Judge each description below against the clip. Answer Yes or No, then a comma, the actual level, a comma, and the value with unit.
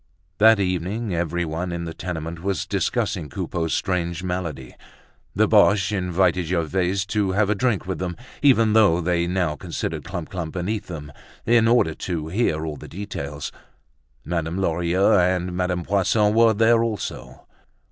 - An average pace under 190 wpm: Yes, average, 150 wpm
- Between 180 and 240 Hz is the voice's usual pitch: No, very low, 90 Hz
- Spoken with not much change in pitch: No, average, 3.2 semitones